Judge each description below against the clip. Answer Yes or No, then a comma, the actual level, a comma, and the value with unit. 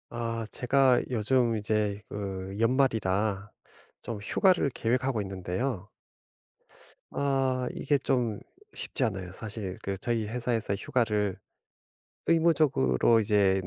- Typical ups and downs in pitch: Yes, average, 4.2 semitones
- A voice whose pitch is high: No, low, 115 Hz